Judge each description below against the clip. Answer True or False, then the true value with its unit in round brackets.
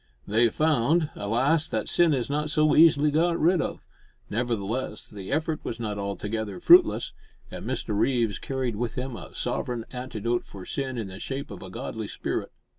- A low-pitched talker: True (125 Hz)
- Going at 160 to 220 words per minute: True (175 wpm)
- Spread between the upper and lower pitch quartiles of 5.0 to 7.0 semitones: True (5.6 semitones)